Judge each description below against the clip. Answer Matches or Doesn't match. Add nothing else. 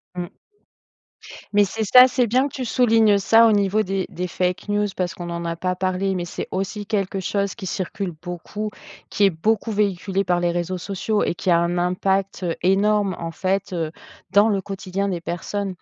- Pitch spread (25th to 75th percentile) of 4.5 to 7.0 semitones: Doesn't match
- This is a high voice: Matches